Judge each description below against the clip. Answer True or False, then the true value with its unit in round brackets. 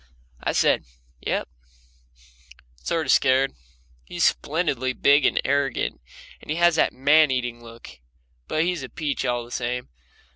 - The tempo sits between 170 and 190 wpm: False (140 wpm)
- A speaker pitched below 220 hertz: True (135 Hz)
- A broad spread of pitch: False (4.0 semitones)